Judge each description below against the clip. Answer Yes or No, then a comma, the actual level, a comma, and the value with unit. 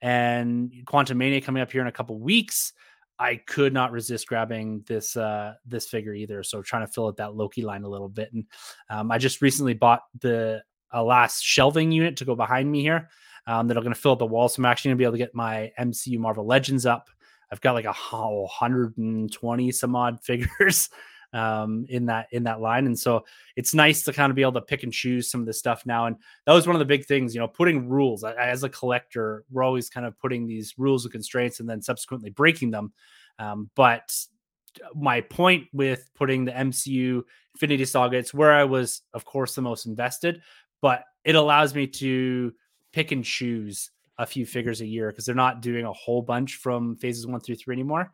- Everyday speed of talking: No, fast, 225 wpm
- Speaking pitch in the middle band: No, low, 125 Hz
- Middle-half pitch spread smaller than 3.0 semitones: Yes, narrow, 2.5 semitones